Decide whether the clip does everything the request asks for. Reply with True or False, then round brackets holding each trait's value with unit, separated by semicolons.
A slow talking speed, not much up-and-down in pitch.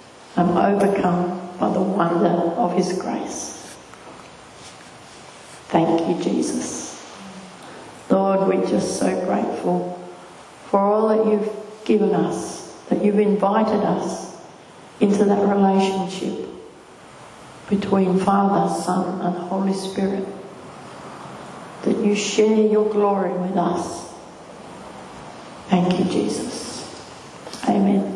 True (100 wpm; 2.2 semitones)